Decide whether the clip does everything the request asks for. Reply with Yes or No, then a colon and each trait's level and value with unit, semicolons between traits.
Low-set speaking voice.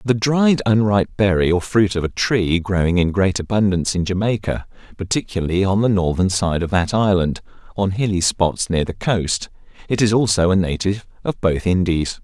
Yes: very low, 95 Hz